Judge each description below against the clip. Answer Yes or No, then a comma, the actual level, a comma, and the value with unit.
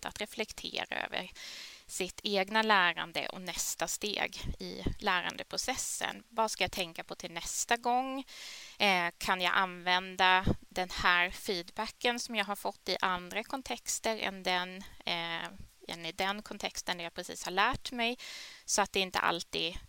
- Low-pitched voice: No, high, 195 Hz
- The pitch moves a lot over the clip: No, average, 3.6 semitones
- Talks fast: No, average, 150 wpm